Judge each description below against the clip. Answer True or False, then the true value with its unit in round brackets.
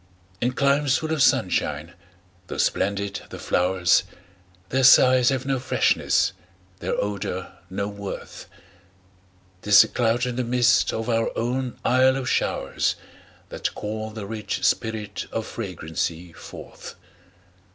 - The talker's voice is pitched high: False (115 Hz)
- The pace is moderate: False (130 wpm)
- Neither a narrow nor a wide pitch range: True (4.2 semitones)